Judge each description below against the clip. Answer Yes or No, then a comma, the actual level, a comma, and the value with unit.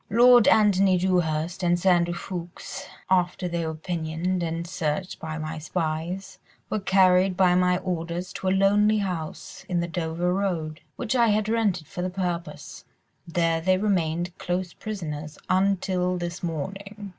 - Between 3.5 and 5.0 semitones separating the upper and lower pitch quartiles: No, narrow, 2.4 semitones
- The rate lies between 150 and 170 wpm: Yes, average, 155 wpm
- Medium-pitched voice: Yes, medium, 180 Hz